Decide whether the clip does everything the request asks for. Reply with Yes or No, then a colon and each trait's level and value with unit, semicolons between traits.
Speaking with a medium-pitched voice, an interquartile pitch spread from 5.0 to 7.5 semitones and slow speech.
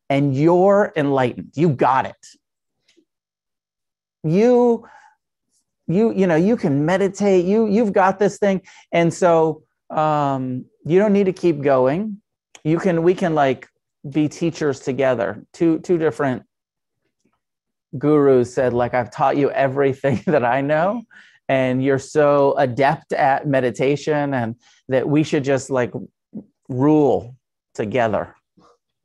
Yes: medium, 150 Hz; average, 5.3 semitones; slow, 130 wpm